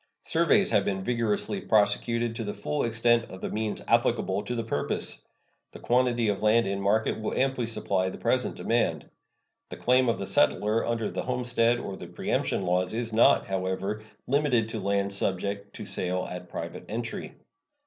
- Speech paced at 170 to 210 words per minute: Yes, average, 175 wpm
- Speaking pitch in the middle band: No, low, 110 Hz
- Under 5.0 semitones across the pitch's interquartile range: Yes, average, 3.1 semitones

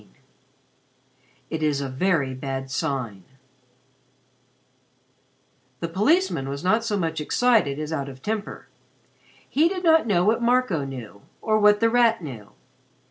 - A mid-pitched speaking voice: Yes, medium, 165 Hz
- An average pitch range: No, wide, 8.6 semitones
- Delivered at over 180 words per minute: No, slow, 135 wpm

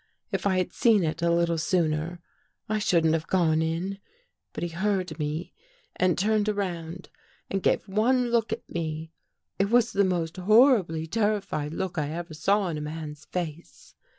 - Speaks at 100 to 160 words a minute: No, average, 170 wpm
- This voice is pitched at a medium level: Yes, medium, 175 Hz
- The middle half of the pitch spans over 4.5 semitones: No, average, 3.9 semitones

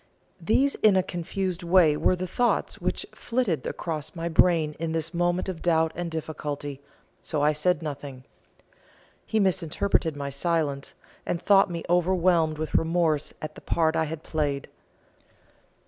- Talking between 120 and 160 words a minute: Yes, average, 150 wpm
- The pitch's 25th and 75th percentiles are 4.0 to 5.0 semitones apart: No, average, 2.7 semitones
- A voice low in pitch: No, medium, 165 Hz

